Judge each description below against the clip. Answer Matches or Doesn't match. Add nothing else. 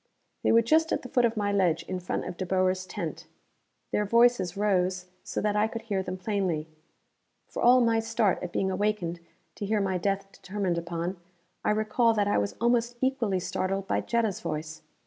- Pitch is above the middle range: Matches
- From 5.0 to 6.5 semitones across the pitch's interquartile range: Doesn't match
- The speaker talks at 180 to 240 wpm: Matches